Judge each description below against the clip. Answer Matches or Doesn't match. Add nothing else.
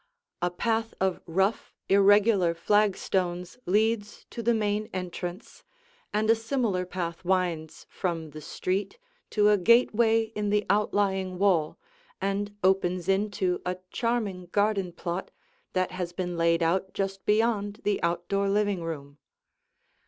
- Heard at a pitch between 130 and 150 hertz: Doesn't match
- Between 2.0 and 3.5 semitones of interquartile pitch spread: Matches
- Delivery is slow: Matches